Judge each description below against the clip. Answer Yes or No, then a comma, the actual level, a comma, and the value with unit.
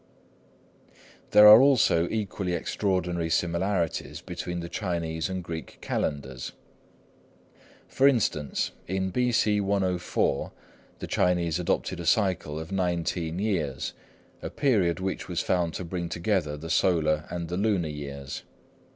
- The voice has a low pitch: Yes, very low, 90 Hz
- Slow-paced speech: Yes, slow, 125 wpm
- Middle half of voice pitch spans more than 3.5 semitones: No, average, 3.0 semitones